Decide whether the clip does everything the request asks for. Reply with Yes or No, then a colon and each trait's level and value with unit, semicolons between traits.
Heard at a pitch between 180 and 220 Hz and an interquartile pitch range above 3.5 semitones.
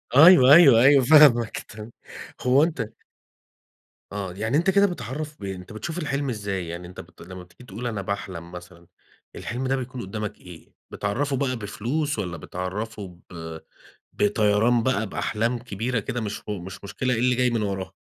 No: low, 110 Hz; average, 5.2 semitones